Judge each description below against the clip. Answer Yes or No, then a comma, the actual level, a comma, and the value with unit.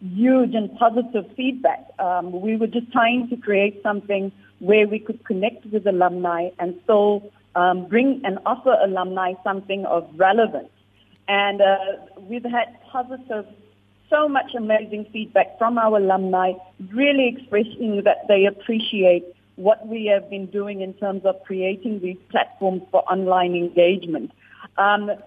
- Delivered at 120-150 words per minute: Yes, average, 140 wpm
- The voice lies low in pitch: No, high, 205 Hz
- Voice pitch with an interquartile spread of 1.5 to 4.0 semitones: Yes, average, 3.1 semitones